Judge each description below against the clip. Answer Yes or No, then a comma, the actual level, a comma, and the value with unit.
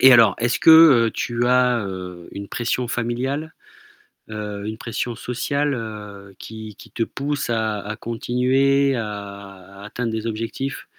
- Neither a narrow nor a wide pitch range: Yes, average, 3.3 semitones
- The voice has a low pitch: Yes, low, 115 Hz